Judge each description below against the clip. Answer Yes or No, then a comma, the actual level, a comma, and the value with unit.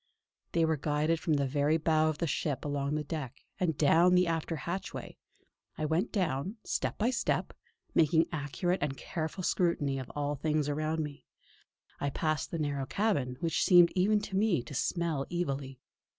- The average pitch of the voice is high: No, medium, 155 Hz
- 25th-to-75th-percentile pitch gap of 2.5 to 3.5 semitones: Yes, average, 3.2 semitones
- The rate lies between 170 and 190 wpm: Yes, average, 180 wpm